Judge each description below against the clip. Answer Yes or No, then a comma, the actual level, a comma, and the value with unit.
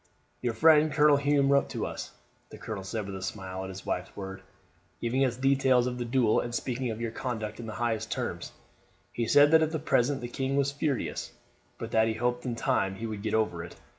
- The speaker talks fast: Yes, fast, 225 wpm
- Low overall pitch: Yes, low, 120 Hz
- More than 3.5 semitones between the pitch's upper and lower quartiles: Yes, average, 3.9 semitones